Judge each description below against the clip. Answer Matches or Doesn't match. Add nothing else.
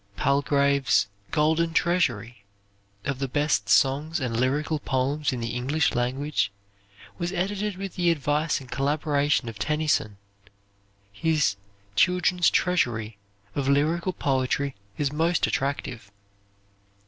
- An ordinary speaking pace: Doesn't match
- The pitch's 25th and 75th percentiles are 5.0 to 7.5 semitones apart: Doesn't match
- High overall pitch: Doesn't match